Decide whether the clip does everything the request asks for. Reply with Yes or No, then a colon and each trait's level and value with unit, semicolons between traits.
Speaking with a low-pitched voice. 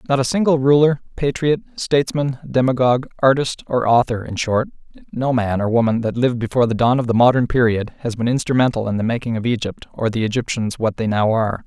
Yes: low, 125 Hz